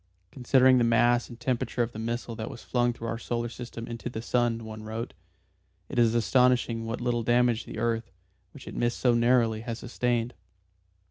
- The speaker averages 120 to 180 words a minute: No, average, 195 wpm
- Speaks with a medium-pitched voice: No, low, 120 Hz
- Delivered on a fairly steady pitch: Yes, narrow, 1.1 semitones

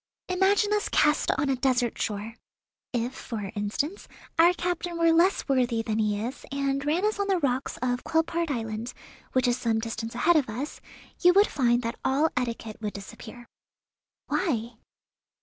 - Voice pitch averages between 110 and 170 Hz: No, very high, 255 Hz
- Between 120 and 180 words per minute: Yes, average, 165 wpm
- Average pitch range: No, wide, 6.4 semitones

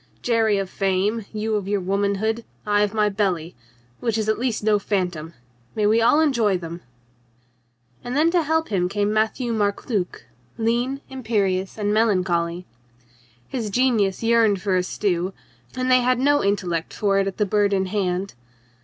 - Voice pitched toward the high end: Yes, high, 205 Hz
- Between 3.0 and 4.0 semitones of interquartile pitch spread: Yes, average, 3.5 semitones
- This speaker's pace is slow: No, average, 175 wpm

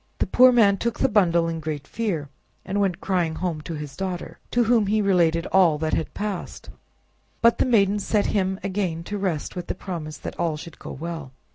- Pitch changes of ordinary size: Yes, average, 4.0 semitones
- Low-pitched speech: No, medium, 185 Hz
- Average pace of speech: No, fast, 210 wpm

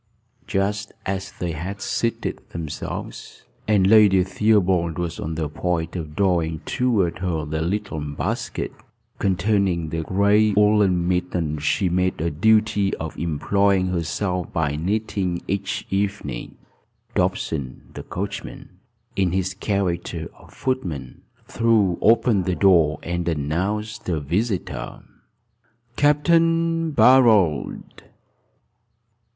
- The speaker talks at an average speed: No, slow, 110 wpm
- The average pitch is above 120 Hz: No, very low, 95 Hz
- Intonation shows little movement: No, average, 3.8 semitones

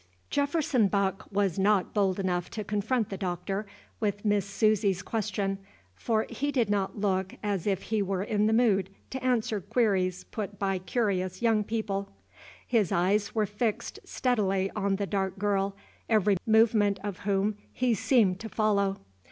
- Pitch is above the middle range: Yes, high, 205 Hz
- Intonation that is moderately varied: No, narrow, 2.1 semitones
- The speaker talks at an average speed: Yes, average, 160 wpm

